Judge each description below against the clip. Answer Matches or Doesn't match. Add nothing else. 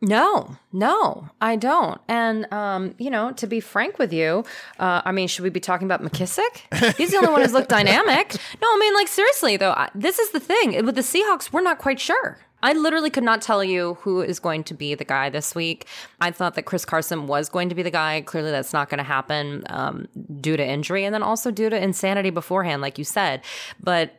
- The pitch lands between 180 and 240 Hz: Matches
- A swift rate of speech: Matches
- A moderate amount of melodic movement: Doesn't match